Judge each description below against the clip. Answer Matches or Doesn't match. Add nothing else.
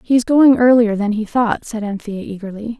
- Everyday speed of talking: Matches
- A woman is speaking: Matches